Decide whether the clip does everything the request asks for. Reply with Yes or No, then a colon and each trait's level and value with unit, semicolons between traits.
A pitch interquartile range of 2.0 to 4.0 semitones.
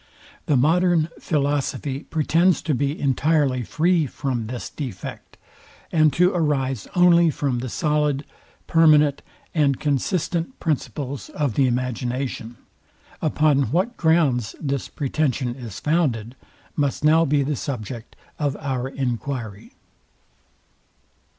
Yes: average, 3.5 semitones